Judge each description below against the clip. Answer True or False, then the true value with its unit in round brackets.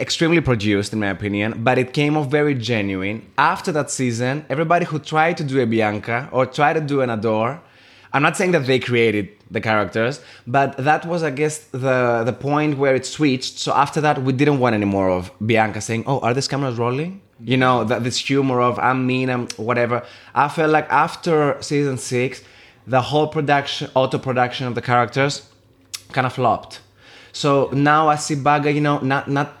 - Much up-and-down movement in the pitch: False (3.7 semitones)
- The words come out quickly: False (195 wpm)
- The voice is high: False (130 Hz)